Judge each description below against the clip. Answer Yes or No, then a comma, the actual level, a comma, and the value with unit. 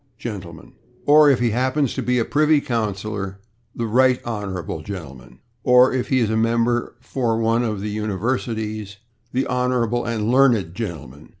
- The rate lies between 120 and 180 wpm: Yes, average, 160 wpm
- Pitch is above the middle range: No, low, 115 Hz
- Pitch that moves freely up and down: No, average, 3.5 semitones